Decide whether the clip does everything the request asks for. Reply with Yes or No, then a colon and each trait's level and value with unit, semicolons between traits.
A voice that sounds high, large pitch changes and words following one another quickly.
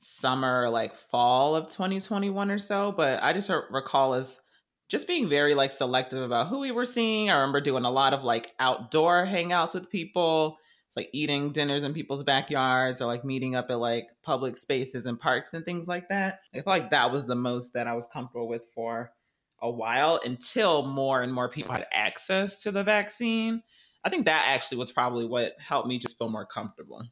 No: low, 135 Hz; wide, 6.2 semitones; fast, 210 wpm